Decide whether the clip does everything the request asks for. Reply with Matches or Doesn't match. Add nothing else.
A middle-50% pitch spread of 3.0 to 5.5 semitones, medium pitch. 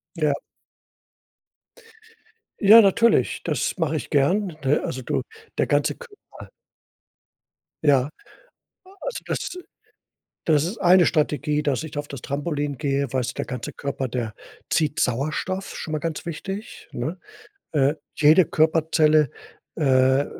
Matches